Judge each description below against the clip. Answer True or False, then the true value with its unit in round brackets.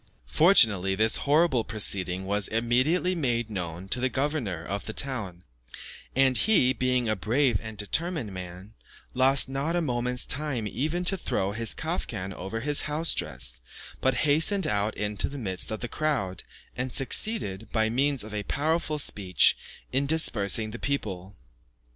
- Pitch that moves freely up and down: True (6.0 semitones)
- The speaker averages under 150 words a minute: False (155 wpm)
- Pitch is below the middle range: True (120 Hz)